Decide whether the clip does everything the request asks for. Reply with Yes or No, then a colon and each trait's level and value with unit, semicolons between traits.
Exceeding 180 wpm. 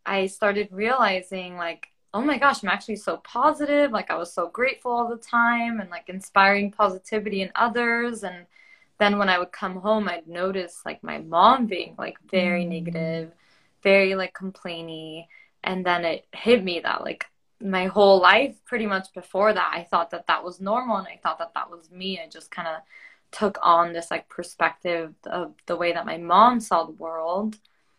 Yes: average, 190 wpm